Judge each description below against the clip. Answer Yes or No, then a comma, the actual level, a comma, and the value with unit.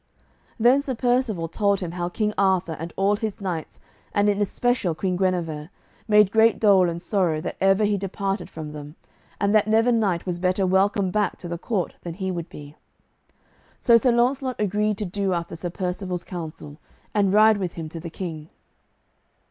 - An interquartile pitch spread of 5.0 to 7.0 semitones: No, average, 3.5 semitones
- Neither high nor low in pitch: No, high, 195 Hz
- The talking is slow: No, average, 185 wpm